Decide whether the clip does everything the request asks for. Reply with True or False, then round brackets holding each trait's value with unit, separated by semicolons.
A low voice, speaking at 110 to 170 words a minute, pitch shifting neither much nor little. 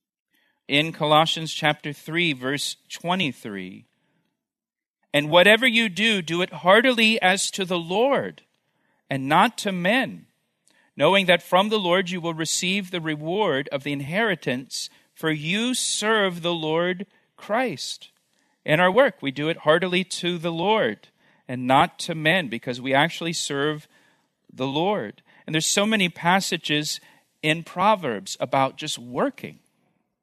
False (175 Hz; 140 wpm; 4.8 semitones)